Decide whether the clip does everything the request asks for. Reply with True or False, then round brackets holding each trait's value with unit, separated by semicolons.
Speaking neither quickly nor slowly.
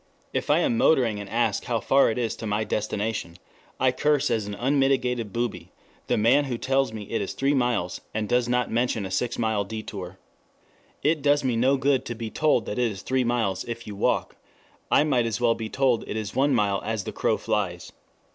False (215 wpm)